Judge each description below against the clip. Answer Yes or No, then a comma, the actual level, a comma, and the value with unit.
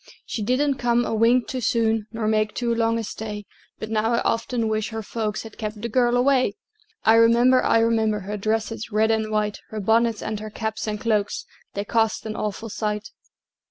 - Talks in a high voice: Yes, high, 220 Hz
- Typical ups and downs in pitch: No, narrow, 1.4 semitones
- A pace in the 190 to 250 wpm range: Yes, average, 200 wpm